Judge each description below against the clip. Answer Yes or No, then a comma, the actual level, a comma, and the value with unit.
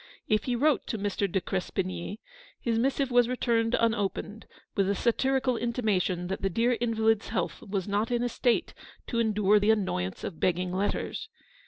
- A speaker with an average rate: Yes, average, 170 wpm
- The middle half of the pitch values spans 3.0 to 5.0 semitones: Yes, average, 3.6 semitones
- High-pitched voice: Yes, high, 220 Hz